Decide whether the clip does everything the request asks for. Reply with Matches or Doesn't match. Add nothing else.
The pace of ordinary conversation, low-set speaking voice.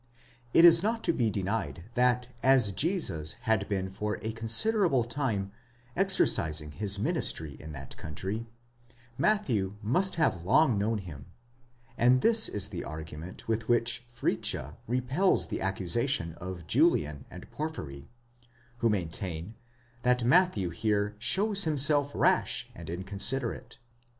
Doesn't match